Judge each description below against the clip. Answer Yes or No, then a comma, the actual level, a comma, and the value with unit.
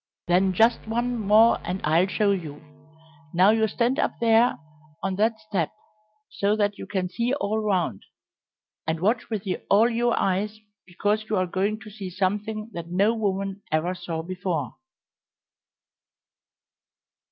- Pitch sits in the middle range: No, high, 200 Hz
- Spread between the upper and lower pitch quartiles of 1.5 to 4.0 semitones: Yes, average, 3.1 semitones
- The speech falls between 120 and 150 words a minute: Yes, average, 145 wpm